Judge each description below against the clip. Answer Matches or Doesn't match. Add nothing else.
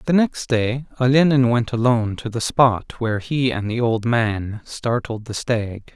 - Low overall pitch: Matches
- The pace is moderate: Matches